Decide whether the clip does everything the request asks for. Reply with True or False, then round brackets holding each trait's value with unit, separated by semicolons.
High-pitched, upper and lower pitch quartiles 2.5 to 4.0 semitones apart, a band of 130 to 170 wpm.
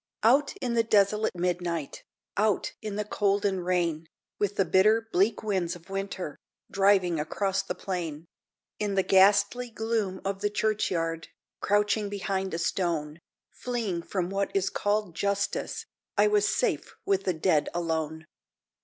True (195 Hz; 3.0 semitones; 145 wpm)